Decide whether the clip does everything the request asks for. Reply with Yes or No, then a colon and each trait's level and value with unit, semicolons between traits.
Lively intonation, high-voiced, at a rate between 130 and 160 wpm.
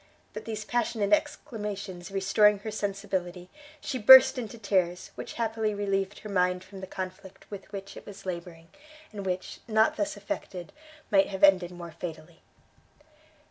No: average, 2.7 semitones; high, 195 Hz; average, 150 wpm